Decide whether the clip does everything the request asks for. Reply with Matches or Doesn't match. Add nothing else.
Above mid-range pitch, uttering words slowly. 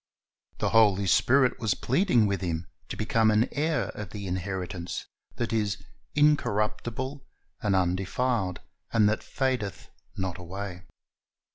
Doesn't match